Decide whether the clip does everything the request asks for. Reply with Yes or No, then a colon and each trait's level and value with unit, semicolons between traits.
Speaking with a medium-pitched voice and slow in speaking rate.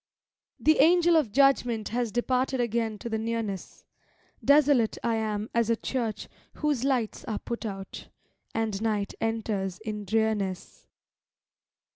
No: high, 225 Hz; slow, 130 wpm